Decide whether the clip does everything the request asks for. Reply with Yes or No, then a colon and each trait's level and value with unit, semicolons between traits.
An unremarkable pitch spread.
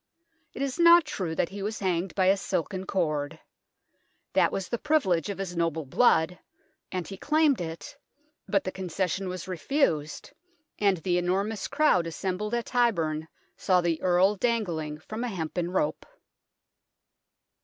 Yes: average, 4.3 semitones